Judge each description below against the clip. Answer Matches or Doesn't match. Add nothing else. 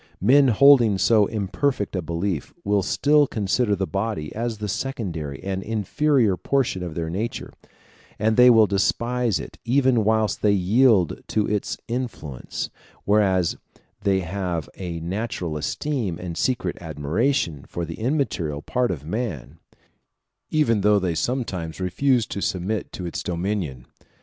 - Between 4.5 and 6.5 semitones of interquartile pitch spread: Matches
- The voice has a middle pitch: Doesn't match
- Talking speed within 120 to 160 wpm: Matches